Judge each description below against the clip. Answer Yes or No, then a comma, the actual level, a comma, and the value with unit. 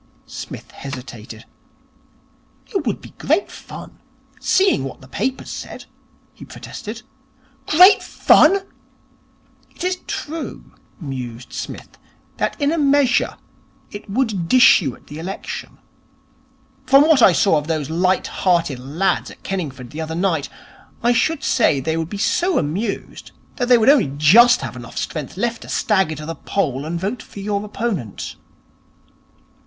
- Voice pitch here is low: No, high, 195 Hz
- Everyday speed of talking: Yes, average, 150 wpm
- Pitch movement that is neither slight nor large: No, wide, 8.6 semitones